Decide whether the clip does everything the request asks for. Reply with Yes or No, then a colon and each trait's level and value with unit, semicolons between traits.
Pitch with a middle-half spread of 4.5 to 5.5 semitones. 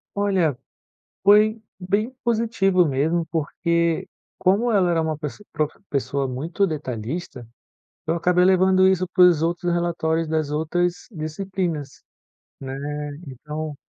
No: average, 3.6 semitones